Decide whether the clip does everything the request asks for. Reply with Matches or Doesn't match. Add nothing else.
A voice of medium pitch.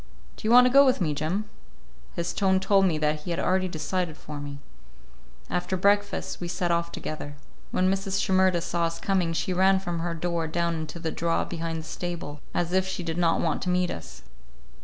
Matches